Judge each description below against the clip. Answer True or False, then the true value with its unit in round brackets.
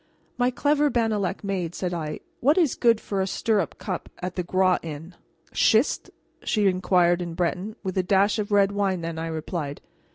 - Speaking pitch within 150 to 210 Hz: True (190 Hz)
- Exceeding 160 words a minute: True (185 wpm)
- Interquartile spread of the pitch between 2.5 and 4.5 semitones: True (3.3 semitones)